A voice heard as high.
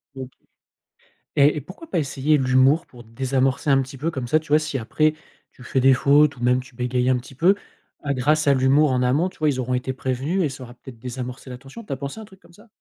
No: low, 135 Hz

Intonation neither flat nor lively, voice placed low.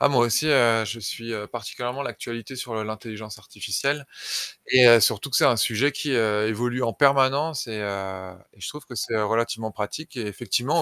Yes: average, 3.5 semitones; low, 115 Hz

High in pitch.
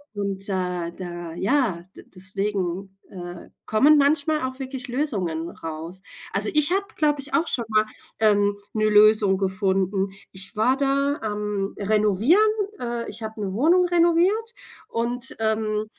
Yes: high, 215 Hz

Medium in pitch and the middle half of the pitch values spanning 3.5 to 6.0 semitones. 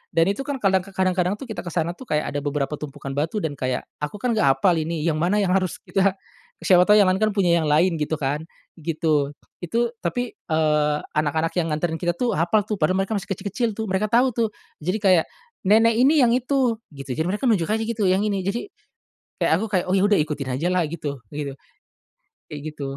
Yes: medium, 175 Hz; average, 5.1 semitones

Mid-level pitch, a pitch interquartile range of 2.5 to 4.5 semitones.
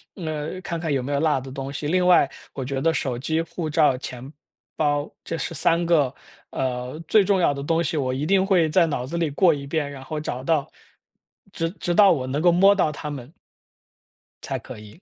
Yes: medium, 155 Hz; average, 3.6 semitones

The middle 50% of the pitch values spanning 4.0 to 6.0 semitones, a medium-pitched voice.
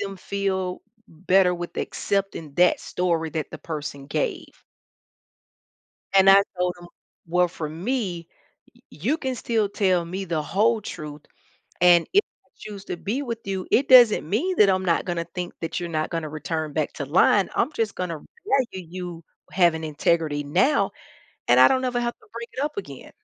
Yes: average, 4.5 semitones; medium, 180 Hz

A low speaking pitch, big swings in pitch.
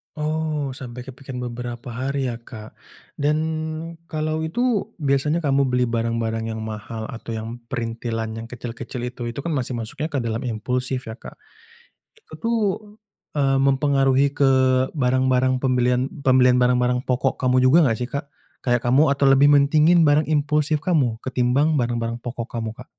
No: low, 130 Hz; average, 3.1 semitones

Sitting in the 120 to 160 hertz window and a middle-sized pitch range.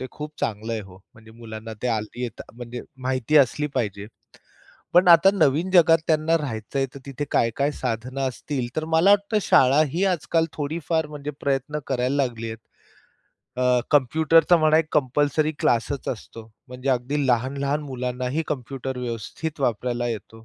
Yes: low, 135 Hz; average, 4.2 semitones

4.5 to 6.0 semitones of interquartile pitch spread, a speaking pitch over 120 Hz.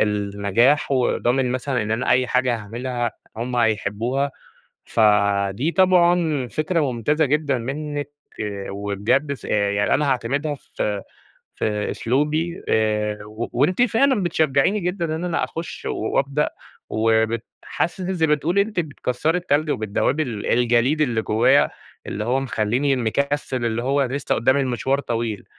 Yes: average, 5.2 semitones; low, 130 Hz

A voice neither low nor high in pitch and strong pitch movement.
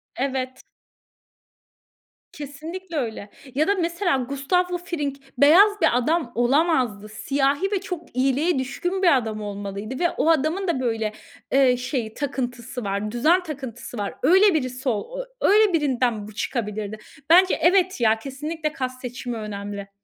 No: very high, 270 Hz; wide, 6.2 semitones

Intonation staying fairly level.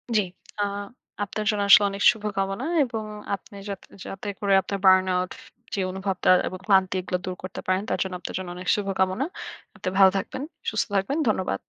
Yes: narrow, 1.7 semitones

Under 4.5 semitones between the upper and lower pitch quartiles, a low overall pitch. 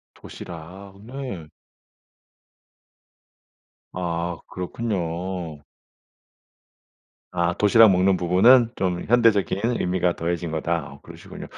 Yes: average, 2.9 semitones; very low, 90 Hz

